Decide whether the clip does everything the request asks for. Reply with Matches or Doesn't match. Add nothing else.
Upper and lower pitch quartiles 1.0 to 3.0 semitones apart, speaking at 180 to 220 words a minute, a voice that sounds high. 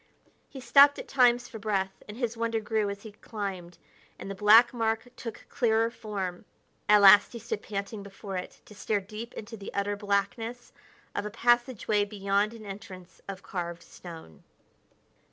Doesn't match